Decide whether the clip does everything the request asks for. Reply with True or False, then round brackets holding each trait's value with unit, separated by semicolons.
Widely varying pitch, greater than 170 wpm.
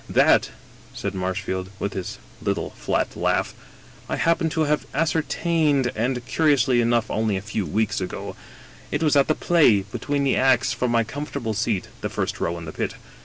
True (6.2 semitones; 180 wpm)